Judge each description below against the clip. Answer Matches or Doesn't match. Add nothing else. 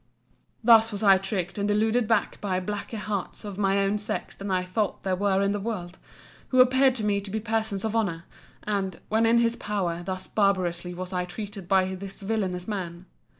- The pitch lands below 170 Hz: Doesn't match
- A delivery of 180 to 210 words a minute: Matches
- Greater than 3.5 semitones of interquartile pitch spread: Doesn't match